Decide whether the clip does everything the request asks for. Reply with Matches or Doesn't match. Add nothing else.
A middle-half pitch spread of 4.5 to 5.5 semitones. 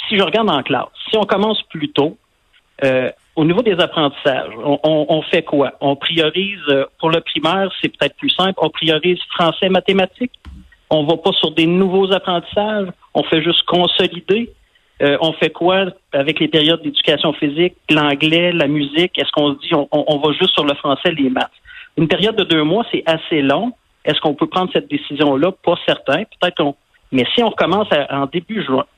Doesn't match